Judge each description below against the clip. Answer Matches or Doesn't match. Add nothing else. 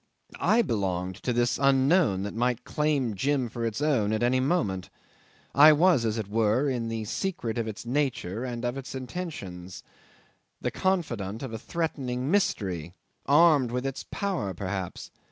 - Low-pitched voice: Matches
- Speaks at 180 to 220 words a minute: Doesn't match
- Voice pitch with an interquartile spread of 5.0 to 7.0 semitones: Matches